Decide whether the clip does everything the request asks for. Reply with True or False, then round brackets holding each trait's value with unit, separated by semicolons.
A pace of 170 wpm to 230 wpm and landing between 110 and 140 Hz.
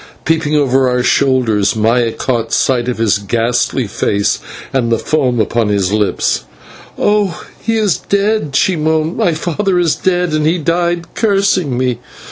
False (155 wpm; 135 Hz)